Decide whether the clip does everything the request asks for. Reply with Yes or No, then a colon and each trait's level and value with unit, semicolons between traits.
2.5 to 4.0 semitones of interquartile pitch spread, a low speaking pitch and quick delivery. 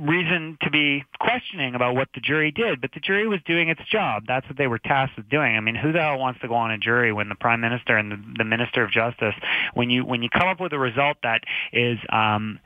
No: average, 4.9 semitones; low, 130 Hz; fast, 265 wpm